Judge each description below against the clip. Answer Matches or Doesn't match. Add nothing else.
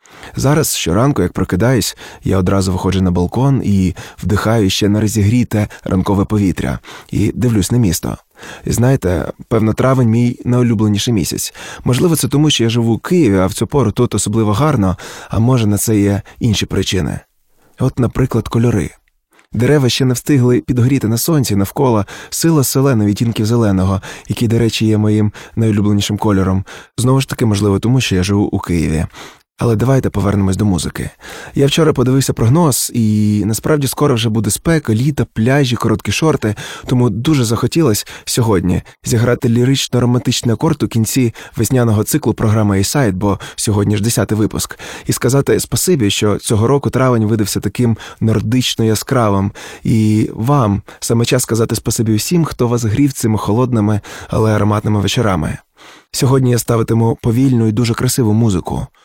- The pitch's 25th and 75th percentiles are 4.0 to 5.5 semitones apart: Doesn't match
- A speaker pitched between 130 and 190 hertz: Doesn't match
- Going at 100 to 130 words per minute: Doesn't match